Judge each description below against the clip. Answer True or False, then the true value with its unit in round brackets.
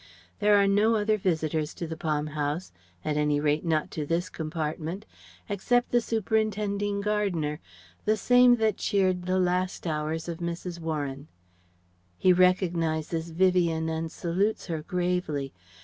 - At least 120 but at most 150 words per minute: True (140 wpm)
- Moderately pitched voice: True (175 Hz)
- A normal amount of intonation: True (4.2 semitones)